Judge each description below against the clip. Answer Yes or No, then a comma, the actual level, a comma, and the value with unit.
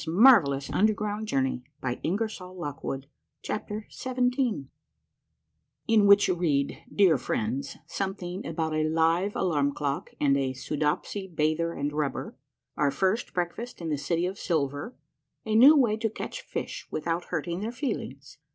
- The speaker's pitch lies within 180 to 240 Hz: No, medium, 170 Hz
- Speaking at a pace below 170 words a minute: Yes, average, 145 wpm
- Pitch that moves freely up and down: Yes, wide, 6.3 semitones